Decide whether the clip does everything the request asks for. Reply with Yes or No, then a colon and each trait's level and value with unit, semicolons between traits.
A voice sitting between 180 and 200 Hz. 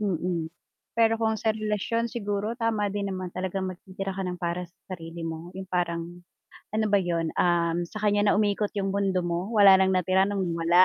Yes: high, 190 Hz